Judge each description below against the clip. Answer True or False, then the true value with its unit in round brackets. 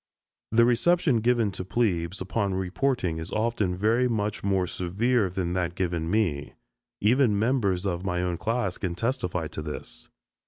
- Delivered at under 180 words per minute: True (155 wpm)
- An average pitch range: True (4.5 semitones)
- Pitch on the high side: False (100 Hz)